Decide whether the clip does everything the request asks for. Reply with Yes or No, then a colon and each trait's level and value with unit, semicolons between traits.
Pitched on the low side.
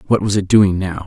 Yes: very low, 95 Hz